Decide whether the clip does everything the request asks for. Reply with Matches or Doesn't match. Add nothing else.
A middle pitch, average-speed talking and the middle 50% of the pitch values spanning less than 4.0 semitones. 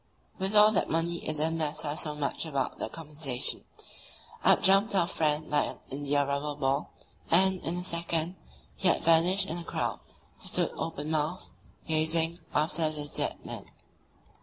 Matches